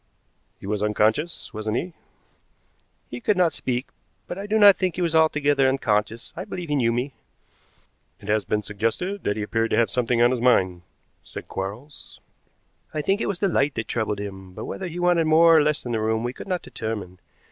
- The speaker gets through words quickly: Yes, fast, 210 wpm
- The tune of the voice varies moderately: No, wide, 7.3 semitones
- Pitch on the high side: No, low, 125 Hz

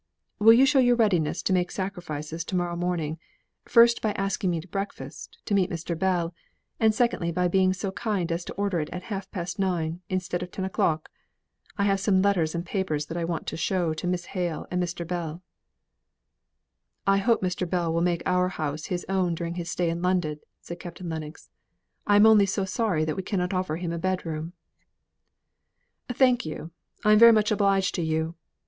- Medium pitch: Yes, medium, 180 Hz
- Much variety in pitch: No, average, 2.7 semitones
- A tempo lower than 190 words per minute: No, average, 195 wpm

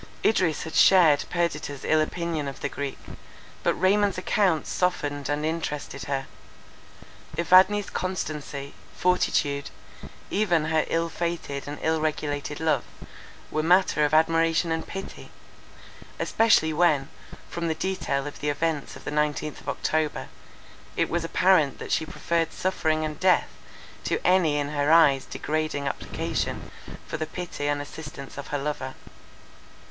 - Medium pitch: Yes, medium, 155 Hz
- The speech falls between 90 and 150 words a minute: Yes, average, 140 wpm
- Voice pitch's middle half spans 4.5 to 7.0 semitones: No, average, 2.9 semitones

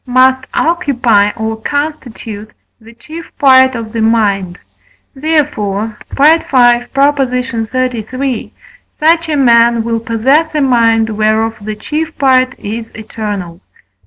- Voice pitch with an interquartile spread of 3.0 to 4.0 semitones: Yes, average, 3.7 semitones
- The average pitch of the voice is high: Yes, high, 240 Hz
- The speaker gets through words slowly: Yes, slow, 110 wpm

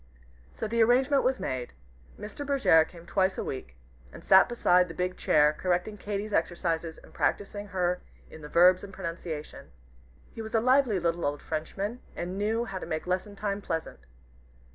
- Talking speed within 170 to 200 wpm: Yes, average, 175 wpm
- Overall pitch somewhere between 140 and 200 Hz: Yes, medium, 185 Hz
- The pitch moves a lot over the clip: No, average, 4.2 semitones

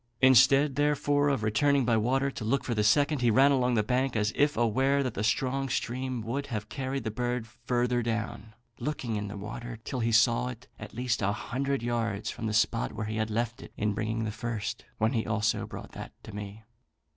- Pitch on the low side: Yes, low, 120 Hz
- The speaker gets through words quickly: Yes, fast, 215 wpm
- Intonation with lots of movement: No, average, 3.3 semitones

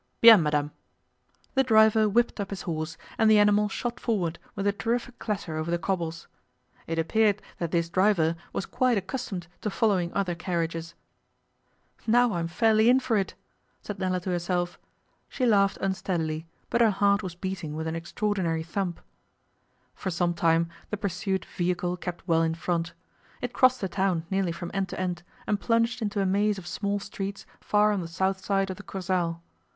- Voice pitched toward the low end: No, high, 190 Hz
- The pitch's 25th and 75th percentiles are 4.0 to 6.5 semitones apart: No, average, 3.5 semitones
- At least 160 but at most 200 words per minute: Yes, average, 180 wpm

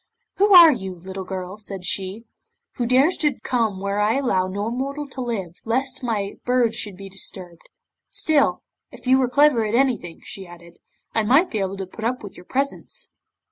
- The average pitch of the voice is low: No, high, 220 Hz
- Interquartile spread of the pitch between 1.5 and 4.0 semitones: No, average, 5.3 semitones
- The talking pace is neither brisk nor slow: Yes, average, 190 wpm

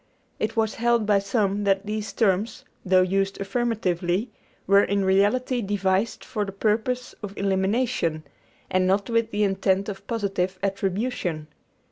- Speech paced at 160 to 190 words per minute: No, average, 140 wpm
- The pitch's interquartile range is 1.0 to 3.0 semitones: Yes, narrow, 2.6 semitones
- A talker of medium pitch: No, high, 200 Hz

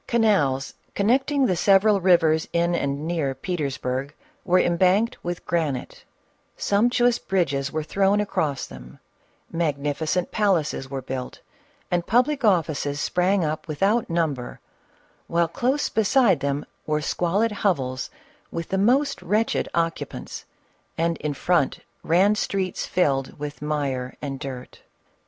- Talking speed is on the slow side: Yes, slow, 125 wpm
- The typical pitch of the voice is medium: Yes, medium, 170 Hz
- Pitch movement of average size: No, wide, 5.7 semitones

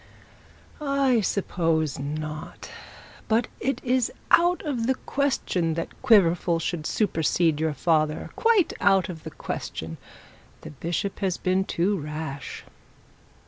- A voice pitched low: No, medium, 175 Hz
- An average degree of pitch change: No, wide, 6.7 semitones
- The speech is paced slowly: Yes, slow, 120 wpm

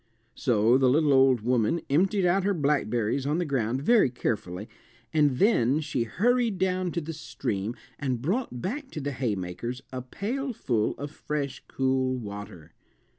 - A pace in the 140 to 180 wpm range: Yes, average, 155 wpm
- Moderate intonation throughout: No, wide, 6.6 semitones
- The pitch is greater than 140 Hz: No, low, 135 Hz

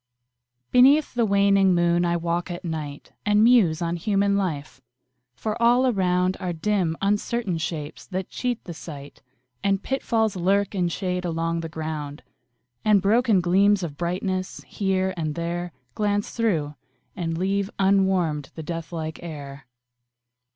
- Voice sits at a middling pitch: Yes, medium, 180 Hz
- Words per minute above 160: No, average, 145 wpm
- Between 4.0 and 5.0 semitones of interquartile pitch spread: No, average, 3.3 semitones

